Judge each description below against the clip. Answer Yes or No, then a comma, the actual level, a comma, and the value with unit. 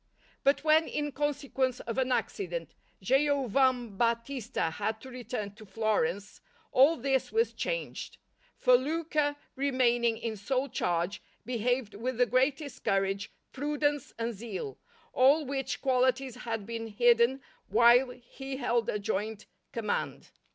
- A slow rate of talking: Yes, slow, 125 wpm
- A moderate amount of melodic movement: Yes, average, 3.4 semitones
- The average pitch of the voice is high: Yes, very high, 250 Hz